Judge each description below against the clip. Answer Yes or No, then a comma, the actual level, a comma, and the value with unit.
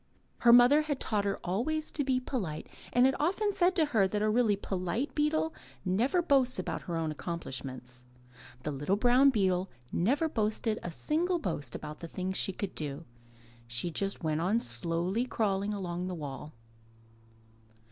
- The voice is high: Yes, high, 205 Hz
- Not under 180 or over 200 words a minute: No, average, 170 wpm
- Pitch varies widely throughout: Yes, wide, 7.3 semitones